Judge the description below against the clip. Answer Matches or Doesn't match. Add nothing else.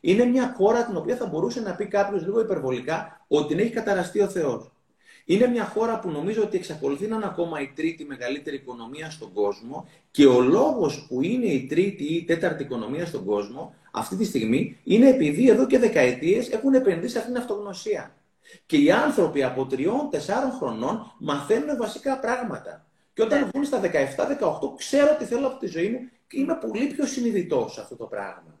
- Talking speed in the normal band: Doesn't match